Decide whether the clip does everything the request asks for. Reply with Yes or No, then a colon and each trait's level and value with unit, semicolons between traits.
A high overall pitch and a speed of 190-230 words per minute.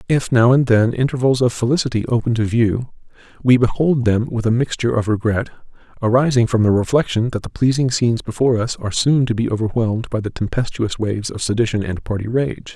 No: low, 115 Hz; average, 200 wpm